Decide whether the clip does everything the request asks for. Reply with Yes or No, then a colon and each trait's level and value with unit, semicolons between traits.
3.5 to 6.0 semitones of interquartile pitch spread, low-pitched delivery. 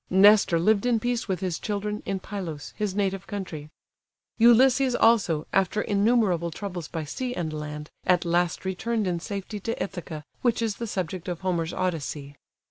No: average, 3.9 semitones; high, 190 Hz